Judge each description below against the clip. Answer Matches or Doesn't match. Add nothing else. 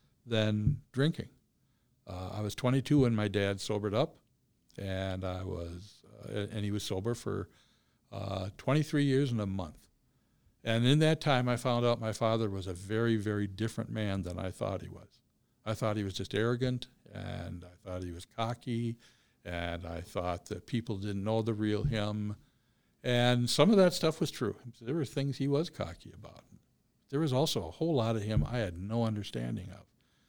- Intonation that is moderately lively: Matches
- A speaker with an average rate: Matches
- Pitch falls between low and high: Doesn't match